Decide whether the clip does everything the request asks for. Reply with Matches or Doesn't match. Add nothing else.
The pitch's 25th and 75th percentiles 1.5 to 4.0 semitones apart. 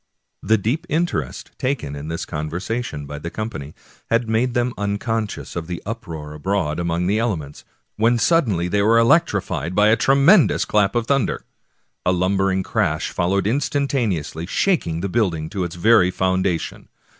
Doesn't match